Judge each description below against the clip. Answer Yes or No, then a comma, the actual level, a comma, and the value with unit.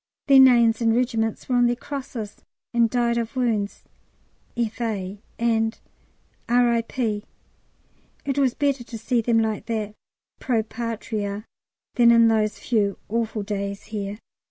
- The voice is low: No, high, 230 Hz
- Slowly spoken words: Yes, slow, 130 wpm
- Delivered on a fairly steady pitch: Yes, narrow, 2.1 semitones